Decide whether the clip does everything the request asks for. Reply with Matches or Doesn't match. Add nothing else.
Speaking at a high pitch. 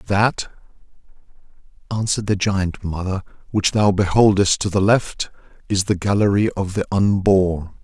Doesn't match